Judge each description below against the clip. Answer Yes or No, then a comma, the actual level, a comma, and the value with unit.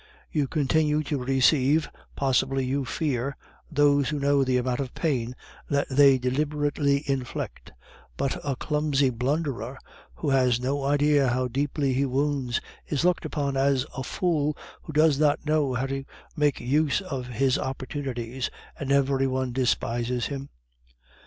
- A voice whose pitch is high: No, medium, 140 Hz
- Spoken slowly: No, average, 145 wpm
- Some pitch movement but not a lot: No, narrow, 2.1 semitones